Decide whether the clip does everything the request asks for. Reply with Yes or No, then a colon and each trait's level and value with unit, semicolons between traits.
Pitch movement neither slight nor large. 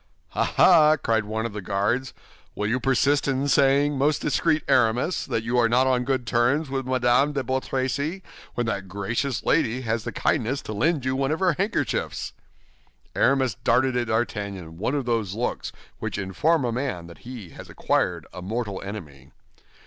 Yes: average, 4.0 semitones